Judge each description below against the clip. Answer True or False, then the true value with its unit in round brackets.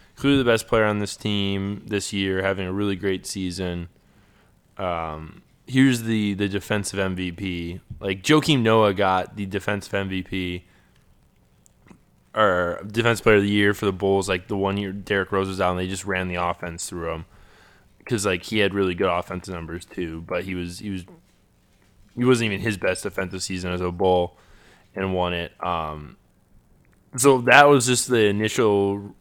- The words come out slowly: False (175 wpm)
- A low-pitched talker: True (95 Hz)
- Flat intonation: True (2.3 semitones)